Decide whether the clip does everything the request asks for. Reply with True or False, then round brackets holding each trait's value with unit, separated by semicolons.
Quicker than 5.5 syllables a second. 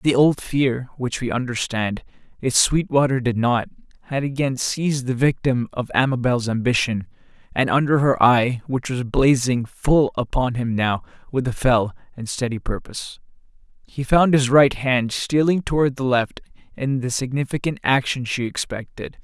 False (4.7 syllables/s)